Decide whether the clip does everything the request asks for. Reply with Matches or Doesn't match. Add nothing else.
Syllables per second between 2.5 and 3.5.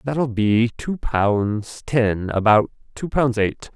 Matches